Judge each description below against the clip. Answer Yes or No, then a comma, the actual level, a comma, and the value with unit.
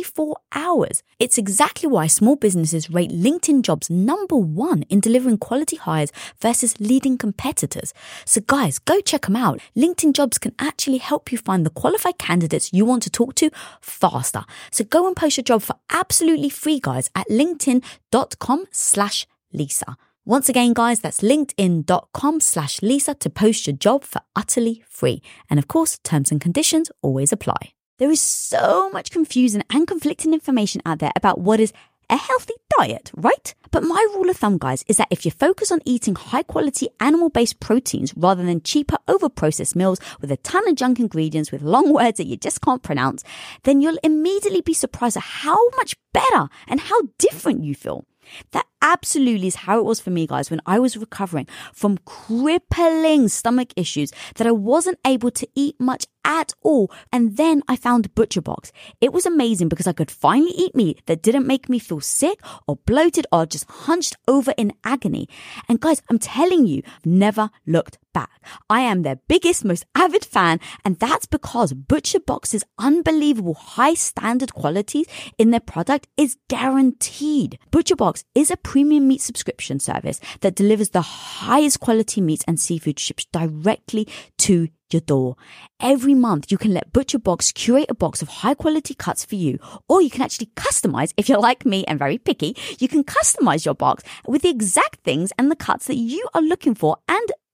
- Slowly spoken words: No, average, 185 wpm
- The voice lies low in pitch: No, high, 240 Hz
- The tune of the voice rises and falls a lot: Yes, wide, 7.9 semitones